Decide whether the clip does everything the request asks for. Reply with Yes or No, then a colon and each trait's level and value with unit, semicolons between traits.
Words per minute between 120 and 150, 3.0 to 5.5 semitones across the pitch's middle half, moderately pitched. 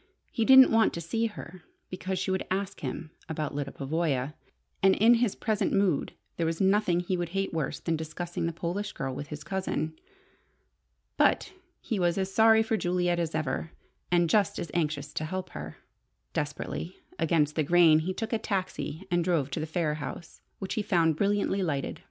No: average, 185 wpm; average, 3.7 semitones; medium, 175 Hz